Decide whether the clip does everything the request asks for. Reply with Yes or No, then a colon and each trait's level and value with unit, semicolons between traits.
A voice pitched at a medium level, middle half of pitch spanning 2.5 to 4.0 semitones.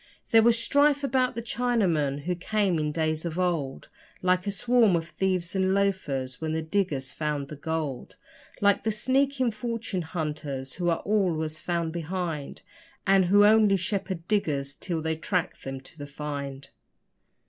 No: medium, 175 Hz; average, 5.1 semitones